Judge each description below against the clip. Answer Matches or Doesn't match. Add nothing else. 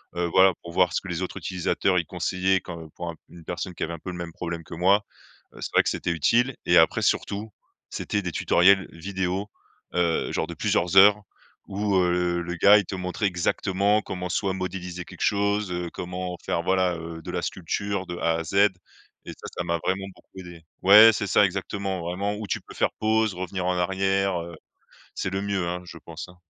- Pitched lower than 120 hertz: Matches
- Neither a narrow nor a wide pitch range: Doesn't match